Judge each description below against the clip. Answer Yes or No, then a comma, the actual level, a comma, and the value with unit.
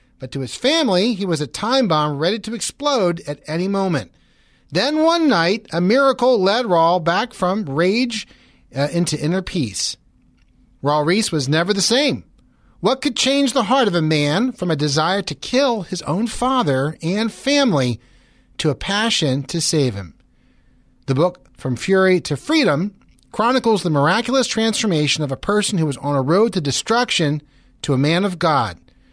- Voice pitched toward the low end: No, medium, 180 Hz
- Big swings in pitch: Yes, wide, 7.3 semitones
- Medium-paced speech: Yes, average, 175 wpm